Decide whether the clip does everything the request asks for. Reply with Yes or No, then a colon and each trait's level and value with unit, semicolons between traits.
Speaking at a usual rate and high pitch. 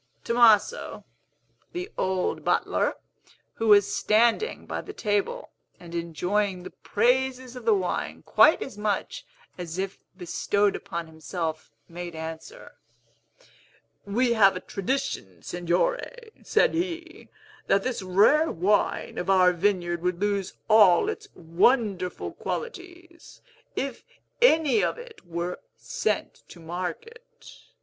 No: slow, 120 wpm; high, 205 Hz